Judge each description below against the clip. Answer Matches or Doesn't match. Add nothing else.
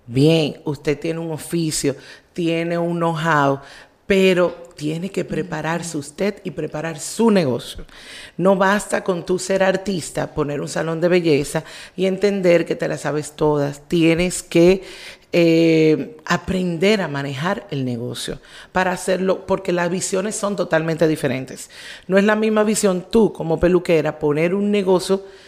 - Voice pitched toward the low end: Doesn't match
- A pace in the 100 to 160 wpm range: Matches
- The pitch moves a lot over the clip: Doesn't match